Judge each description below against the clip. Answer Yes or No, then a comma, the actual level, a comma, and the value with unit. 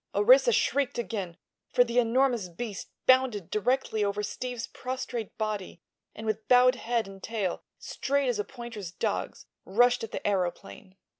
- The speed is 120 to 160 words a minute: Yes, average, 150 wpm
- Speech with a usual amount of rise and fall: Yes, average, 3.4 semitones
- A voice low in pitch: No, high, 230 Hz